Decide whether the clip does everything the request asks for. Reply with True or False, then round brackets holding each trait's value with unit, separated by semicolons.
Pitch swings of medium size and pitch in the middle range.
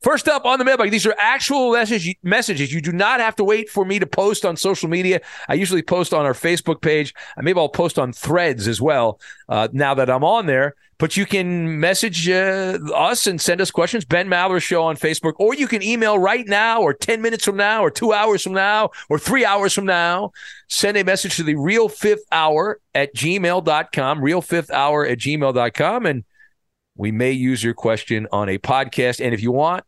False (5.8 semitones; 180 Hz)